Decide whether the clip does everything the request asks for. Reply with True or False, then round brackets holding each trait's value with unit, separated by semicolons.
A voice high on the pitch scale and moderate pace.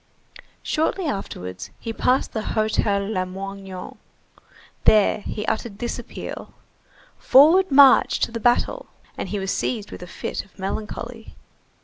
False (215 Hz; 130 wpm)